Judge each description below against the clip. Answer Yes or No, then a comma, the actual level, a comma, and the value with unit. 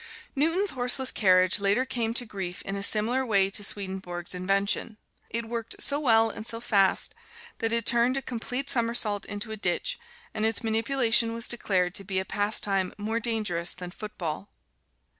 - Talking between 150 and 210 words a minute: Yes, average, 170 wpm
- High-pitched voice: Yes, high, 220 Hz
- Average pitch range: Yes, average, 3.2 semitones